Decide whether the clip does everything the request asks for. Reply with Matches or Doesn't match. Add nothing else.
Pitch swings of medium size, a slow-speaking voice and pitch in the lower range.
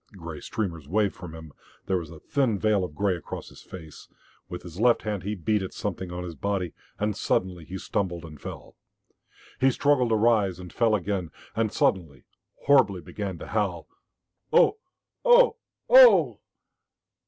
Doesn't match